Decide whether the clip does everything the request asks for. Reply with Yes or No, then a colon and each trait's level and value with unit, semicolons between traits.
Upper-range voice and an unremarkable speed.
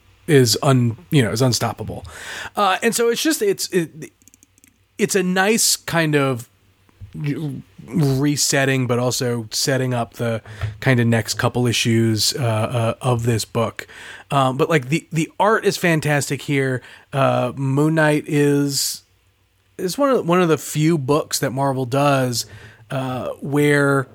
No: low, 135 Hz; average, 150 wpm